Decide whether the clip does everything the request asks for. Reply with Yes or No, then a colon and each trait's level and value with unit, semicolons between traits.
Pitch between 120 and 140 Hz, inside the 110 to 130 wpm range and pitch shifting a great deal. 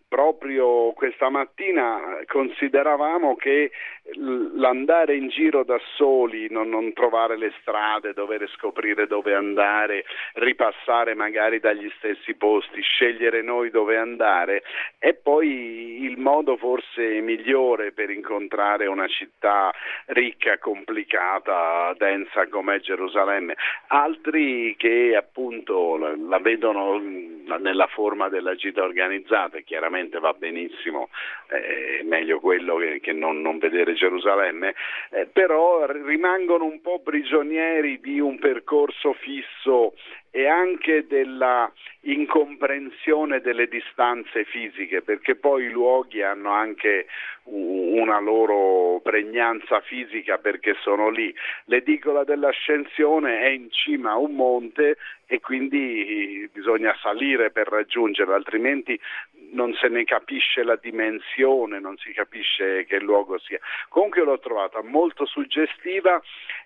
Yes: low, 135 Hz; slow, 115 wpm; wide, 6.2 semitones